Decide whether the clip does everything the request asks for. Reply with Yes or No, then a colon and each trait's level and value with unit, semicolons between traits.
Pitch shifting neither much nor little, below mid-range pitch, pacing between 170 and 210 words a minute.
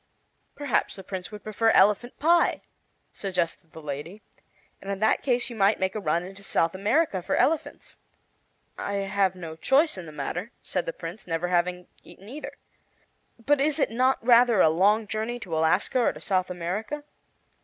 No: average, 4.8 semitones; high, 200 Hz; average, 175 wpm